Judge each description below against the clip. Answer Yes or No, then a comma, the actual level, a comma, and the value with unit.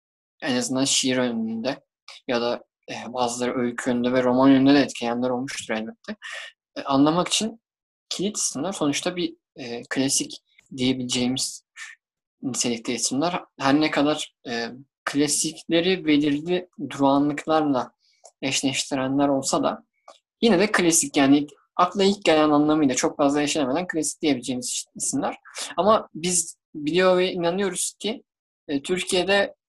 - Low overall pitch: No, medium, 145 Hz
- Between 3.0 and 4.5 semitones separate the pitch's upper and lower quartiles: No, wide, 5.4 semitones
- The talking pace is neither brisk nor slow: Yes, average, 115 wpm